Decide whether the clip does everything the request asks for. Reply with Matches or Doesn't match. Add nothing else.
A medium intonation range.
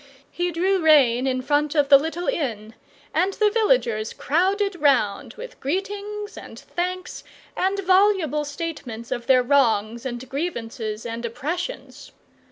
Doesn't match